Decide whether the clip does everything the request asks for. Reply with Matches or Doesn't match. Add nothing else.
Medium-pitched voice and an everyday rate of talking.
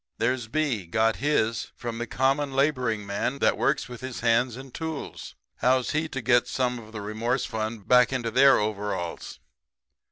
Doesn't match